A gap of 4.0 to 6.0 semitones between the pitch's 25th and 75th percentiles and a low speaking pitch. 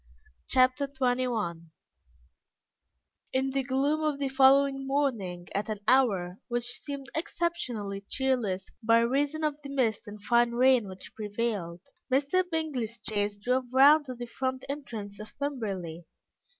No: average, 4.7 semitones; very high, 255 Hz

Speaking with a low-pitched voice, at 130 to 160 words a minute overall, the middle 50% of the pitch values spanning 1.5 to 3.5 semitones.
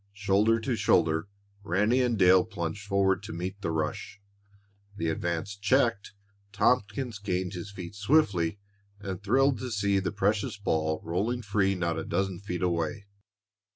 Yes: low, 100 Hz; average, 150 wpm; average, 2.9 semitones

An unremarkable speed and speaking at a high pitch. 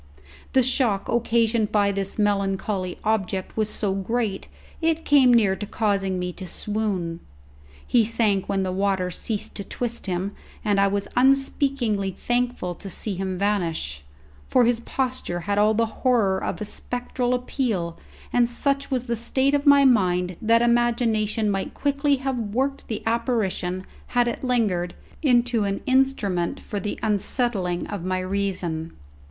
Yes: average, 155 wpm; high, 215 Hz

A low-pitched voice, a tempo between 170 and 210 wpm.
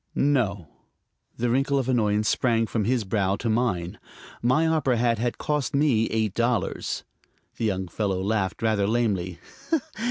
No: low, 115 Hz; average, 150 wpm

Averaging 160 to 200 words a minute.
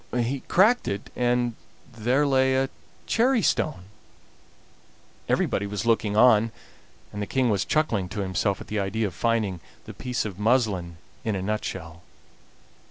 No: average, 150 wpm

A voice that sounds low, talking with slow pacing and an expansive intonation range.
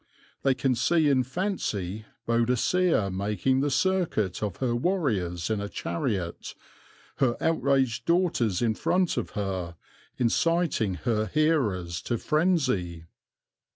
Yes: low, 120 Hz; slow, 120 wpm; wide, 7.6 semitones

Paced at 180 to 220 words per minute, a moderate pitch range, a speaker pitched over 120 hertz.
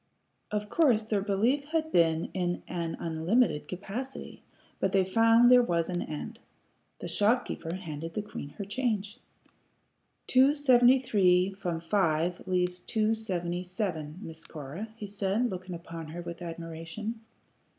No: average, 140 wpm; average, 4.7 semitones; high, 190 Hz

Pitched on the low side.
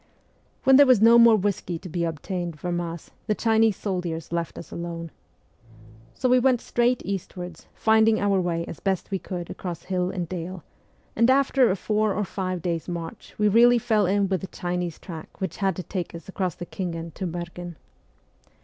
No: medium, 185 Hz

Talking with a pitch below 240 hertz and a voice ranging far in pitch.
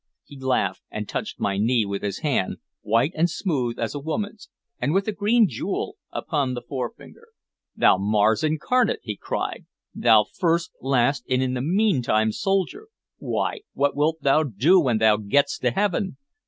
Yes: medium, 140 Hz; wide, 7.8 semitones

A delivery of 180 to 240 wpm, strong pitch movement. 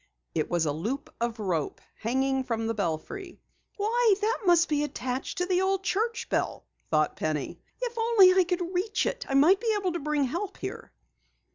Yes: average, 185 wpm; wide, 8.9 semitones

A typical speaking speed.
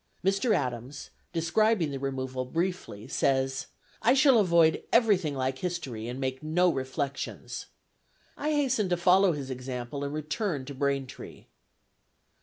No: slow, 130 wpm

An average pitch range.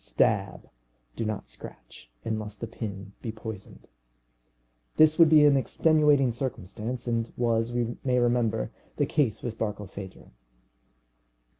Yes: average, 3.0 semitones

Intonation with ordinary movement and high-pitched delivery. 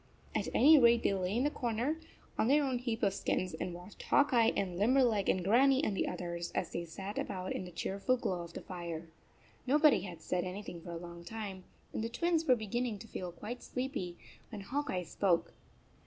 No: wide, 5.7 semitones; high, 205 Hz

